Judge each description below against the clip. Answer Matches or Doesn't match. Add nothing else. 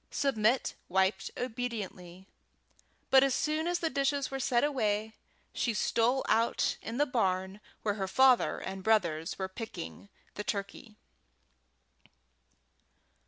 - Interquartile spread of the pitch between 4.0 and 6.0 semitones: Matches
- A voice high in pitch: Matches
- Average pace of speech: Doesn't match